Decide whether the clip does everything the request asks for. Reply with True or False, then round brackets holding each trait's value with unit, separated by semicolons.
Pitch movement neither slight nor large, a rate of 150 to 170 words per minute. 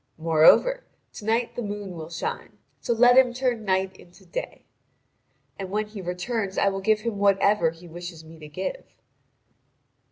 True (4.7 semitones; 165 wpm)